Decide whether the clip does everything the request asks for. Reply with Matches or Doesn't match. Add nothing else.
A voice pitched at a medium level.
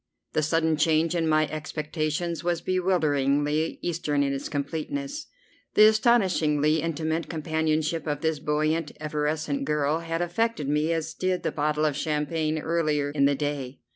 Matches